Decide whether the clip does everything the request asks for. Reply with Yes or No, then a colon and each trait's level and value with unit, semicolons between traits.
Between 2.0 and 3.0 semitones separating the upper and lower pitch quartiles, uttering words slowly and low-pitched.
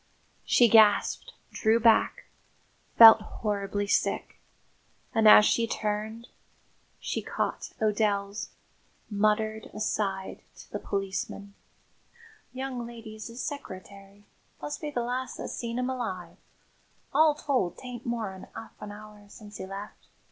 No: narrow, 2.6 semitones; slow, 120 wpm; high, 215 Hz